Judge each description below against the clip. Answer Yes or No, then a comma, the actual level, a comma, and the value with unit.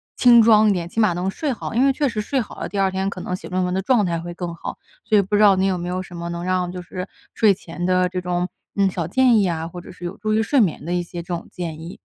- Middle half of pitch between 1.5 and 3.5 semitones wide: Yes, average, 3.2 semitones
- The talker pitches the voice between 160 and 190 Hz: Yes, medium, 185 Hz